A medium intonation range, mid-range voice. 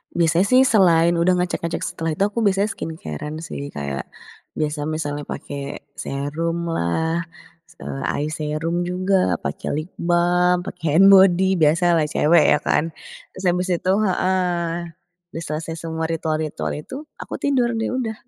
Yes: average, 3.0 semitones; medium, 170 Hz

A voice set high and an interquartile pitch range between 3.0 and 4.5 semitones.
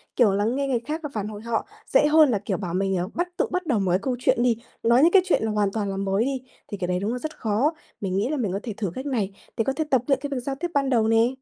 No: high, 235 Hz; average, 5.2 semitones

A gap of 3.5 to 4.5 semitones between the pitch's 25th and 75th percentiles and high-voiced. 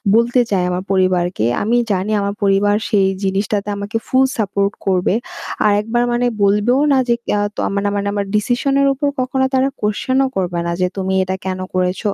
Yes: average, 3.9 semitones; high, 205 Hz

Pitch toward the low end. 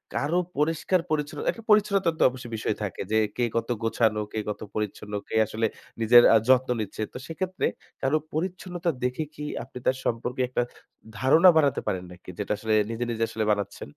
Yes: low, 125 Hz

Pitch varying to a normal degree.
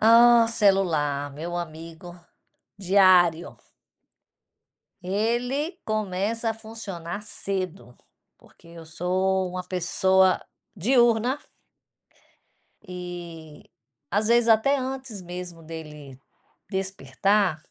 Yes: average, 4.5 semitones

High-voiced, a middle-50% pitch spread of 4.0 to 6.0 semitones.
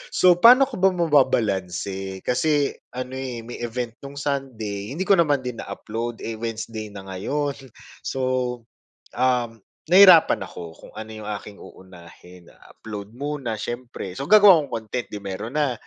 No: low, 120 Hz; wide, 5.5 semitones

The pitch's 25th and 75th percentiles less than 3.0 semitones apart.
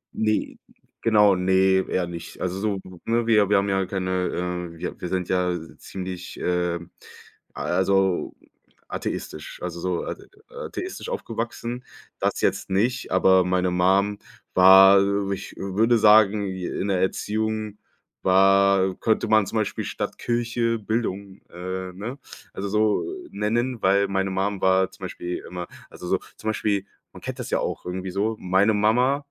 Yes: narrow, 2.6 semitones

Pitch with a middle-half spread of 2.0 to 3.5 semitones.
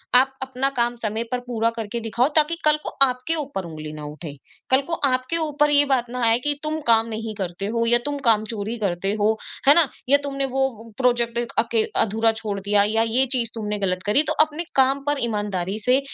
No: average, 4.1 semitones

